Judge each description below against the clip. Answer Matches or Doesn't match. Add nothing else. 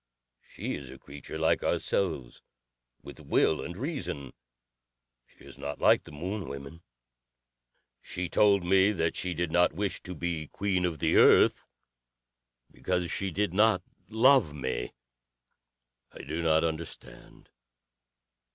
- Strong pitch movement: Doesn't match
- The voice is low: Matches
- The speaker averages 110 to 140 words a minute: Matches